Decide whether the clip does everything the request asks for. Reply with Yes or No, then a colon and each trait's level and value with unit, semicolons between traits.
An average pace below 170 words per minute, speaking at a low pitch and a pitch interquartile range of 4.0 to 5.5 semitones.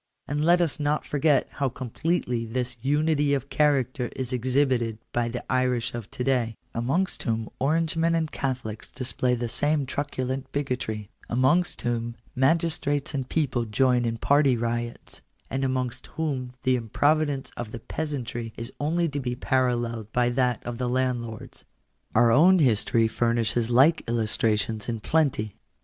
No: average, 150 wpm; low, 130 Hz; average, 3.5 semitones